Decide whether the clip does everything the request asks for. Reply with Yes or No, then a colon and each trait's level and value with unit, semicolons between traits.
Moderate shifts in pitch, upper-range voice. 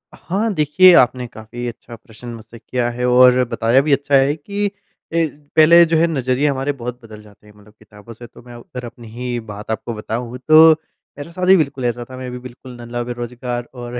No: average, 3.5 semitones; low, 125 Hz